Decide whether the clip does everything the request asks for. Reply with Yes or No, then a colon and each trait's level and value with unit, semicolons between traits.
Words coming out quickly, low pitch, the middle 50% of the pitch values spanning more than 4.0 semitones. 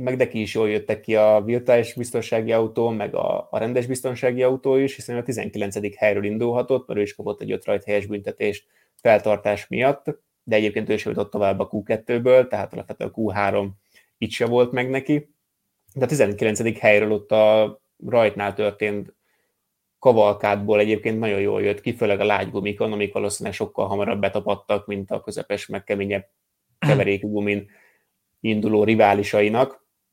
No: fast, 160 wpm; low, 105 Hz; average, 2.8 semitones